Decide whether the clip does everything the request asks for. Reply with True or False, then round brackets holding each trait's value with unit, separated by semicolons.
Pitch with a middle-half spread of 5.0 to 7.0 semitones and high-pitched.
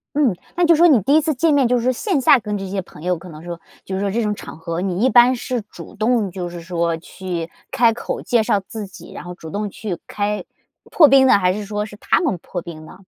True (5.6 semitones; 205 Hz)